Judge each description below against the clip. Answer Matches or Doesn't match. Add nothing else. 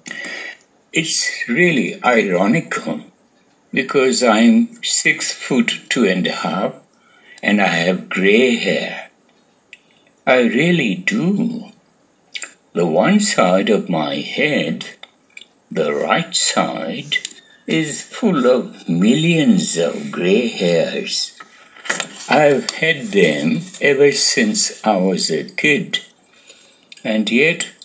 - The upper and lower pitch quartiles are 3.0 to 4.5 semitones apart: Matches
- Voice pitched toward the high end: Matches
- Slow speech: Matches